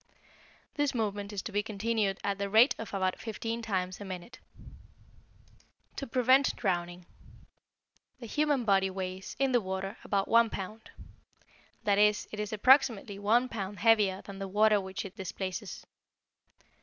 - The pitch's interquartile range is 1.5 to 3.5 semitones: Yes, average, 2.9 semitones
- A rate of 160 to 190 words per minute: No, average, 150 wpm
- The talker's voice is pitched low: No, high, 205 Hz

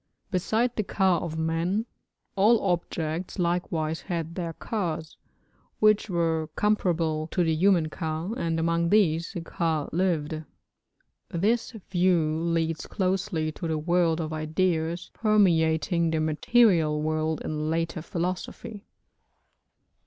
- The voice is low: No, medium, 170 Hz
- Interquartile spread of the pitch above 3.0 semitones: No, average, 2.7 semitones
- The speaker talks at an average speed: No, slow, 120 wpm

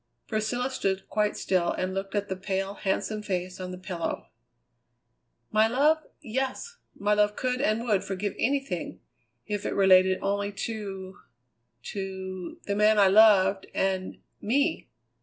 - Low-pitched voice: No, high, 200 Hz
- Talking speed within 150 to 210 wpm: No, average, 140 wpm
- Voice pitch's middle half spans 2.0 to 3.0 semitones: Yes, narrow, 2.4 semitones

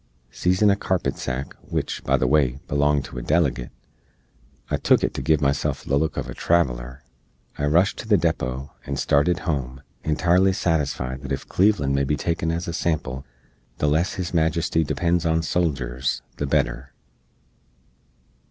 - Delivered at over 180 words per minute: No, average, 165 wpm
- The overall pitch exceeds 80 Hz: No, very low, 75 Hz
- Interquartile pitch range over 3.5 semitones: Yes, average, 4.1 semitones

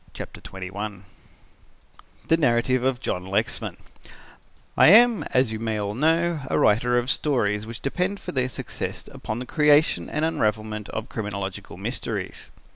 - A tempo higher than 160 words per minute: No, average, 145 wpm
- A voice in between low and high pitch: No, low, 120 Hz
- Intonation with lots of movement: Yes, wide, 6.1 semitones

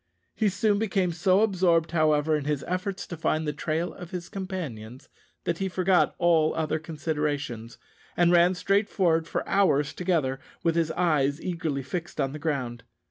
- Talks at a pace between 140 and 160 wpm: No, average, 170 wpm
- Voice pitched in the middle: Yes, medium, 165 Hz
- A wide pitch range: No, average, 3.4 semitones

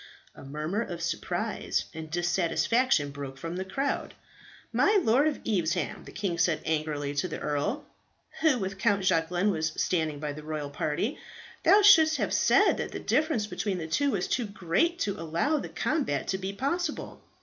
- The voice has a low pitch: No, medium, 185 Hz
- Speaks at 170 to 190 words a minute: Yes, average, 175 wpm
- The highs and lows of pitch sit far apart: Yes, wide, 7.6 semitones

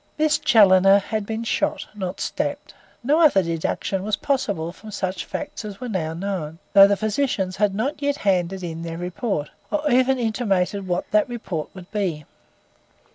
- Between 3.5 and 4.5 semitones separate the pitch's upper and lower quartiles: Yes, average, 4.2 semitones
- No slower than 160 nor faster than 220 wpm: Yes, average, 170 wpm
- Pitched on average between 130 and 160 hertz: No, high, 200 Hz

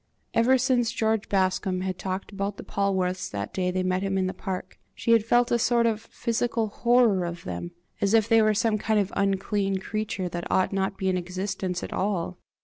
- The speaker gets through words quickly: Yes, fast, 215 wpm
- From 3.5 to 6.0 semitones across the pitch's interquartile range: No, average, 3.0 semitones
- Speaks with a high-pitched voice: Yes, high, 195 Hz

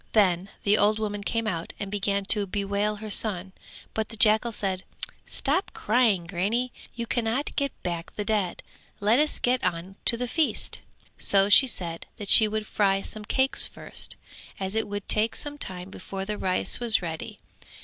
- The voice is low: No, high, 210 Hz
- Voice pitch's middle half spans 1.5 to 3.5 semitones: Yes, average, 2.7 semitones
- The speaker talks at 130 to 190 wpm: Yes, average, 180 wpm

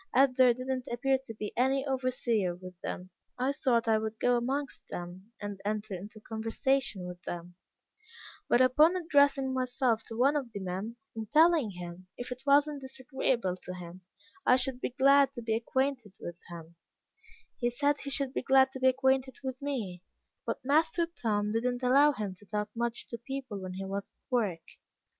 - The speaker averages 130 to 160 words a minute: No, average, 190 wpm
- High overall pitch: Yes, high, 245 Hz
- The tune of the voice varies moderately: Yes, average, 4.5 semitones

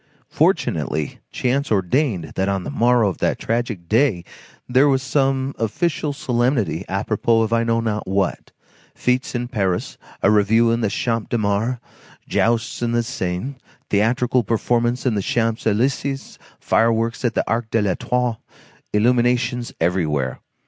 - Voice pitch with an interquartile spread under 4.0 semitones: Yes, average, 3.3 semitones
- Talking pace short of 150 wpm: Yes, average, 140 wpm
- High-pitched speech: No, low, 115 Hz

